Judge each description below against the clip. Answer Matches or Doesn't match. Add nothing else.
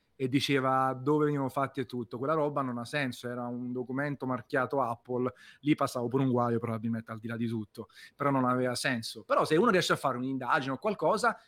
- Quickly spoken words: Matches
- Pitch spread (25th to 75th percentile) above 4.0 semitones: Doesn't match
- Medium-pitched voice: Doesn't match